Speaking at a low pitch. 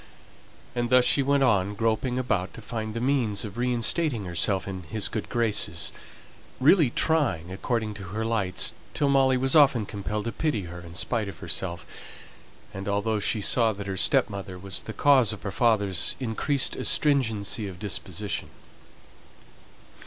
Yes: low, 110 Hz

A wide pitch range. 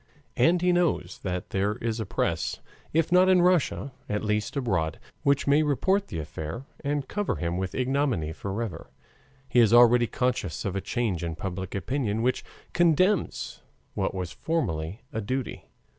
Yes: wide, 7.4 semitones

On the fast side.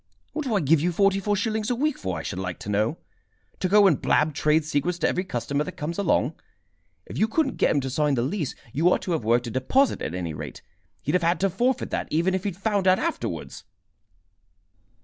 Yes: fast, 235 wpm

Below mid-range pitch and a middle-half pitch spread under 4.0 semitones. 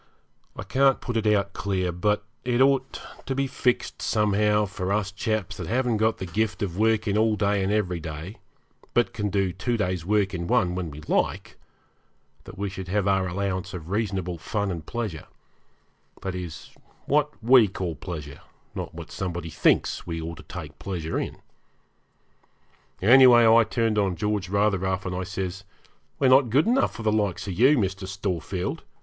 Yes: low, 100 Hz; average, 3.4 semitones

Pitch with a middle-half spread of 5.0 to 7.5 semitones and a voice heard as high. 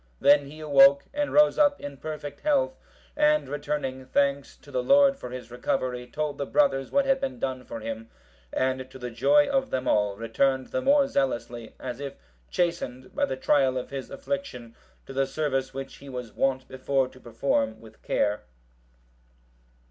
No: wide, 5.5 semitones; low, 135 Hz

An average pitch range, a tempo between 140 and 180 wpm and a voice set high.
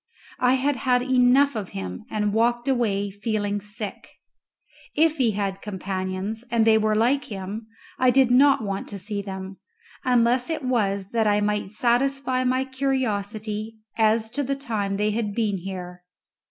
Yes: average, 3.8 semitones; average, 160 wpm; high, 220 Hz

